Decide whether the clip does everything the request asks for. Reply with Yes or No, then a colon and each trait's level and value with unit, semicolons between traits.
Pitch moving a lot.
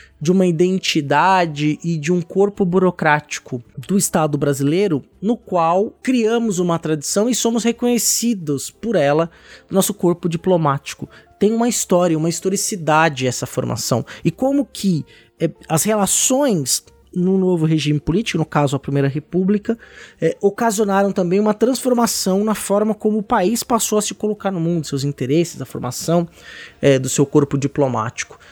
Yes: wide, 5.9 semitones